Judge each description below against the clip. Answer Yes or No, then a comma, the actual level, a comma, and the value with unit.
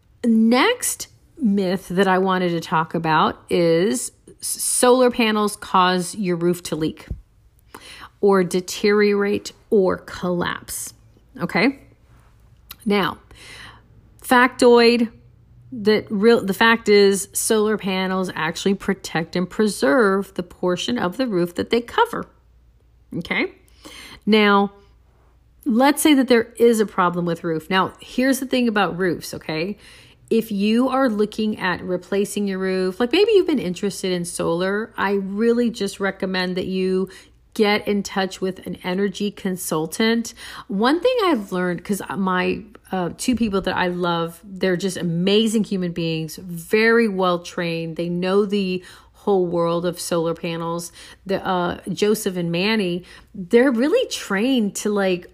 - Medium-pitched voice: No, high, 195 Hz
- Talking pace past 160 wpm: No, slow, 135 wpm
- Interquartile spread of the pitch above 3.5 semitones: Yes, average, 3.9 semitones